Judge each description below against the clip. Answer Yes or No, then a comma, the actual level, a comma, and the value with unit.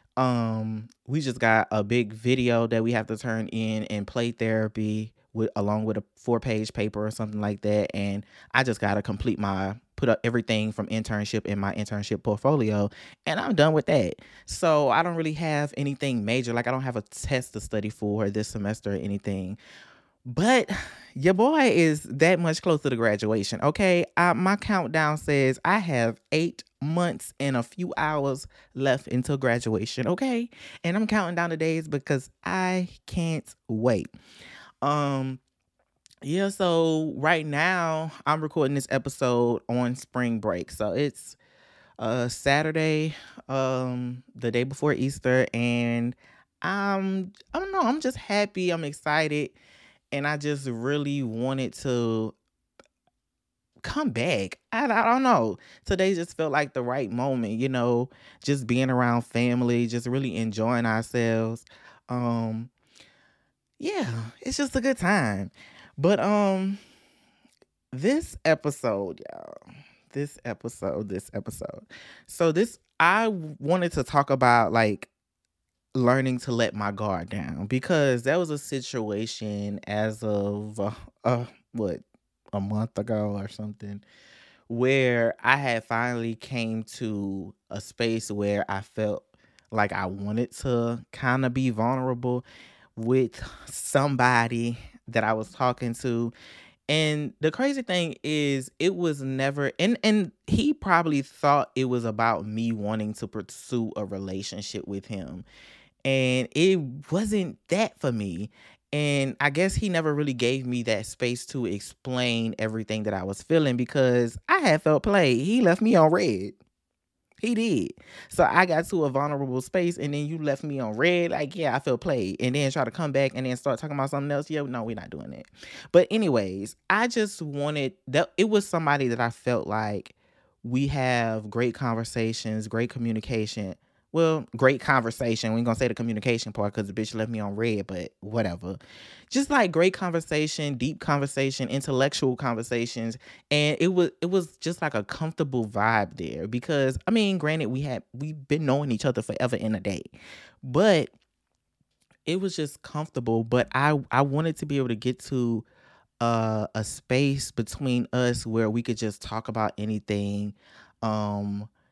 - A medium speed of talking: Yes, average, 160 wpm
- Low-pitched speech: Yes, low, 125 Hz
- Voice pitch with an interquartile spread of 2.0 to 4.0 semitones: No, average, 5.3 semitones